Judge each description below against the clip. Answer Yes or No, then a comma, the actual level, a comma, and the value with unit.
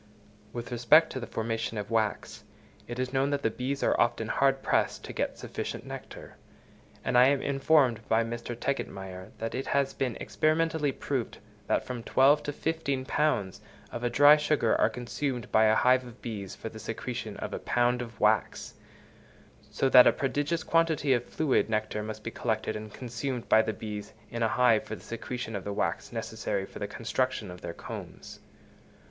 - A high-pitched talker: No, low, 120 Hz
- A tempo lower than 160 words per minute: No, average, 185 wpm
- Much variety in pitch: No, average, 3.8 semitones